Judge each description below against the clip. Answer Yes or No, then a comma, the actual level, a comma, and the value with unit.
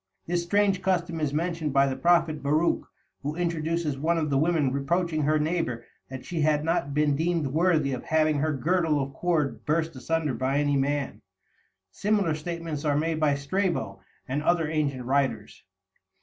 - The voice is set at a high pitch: No, medium, 155 Hz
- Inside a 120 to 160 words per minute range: No, average, 170 wpm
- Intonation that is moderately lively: Yes, average, 3.1 semitones